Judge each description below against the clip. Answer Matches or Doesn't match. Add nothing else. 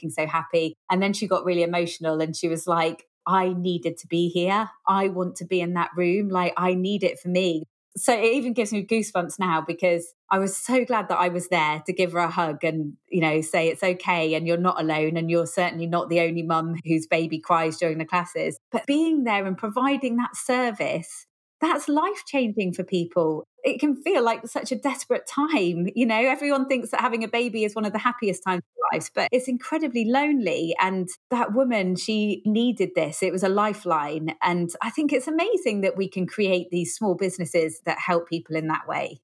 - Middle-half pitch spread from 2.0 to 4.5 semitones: Doesn't match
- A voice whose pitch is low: Doesn't match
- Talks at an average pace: Doesn't match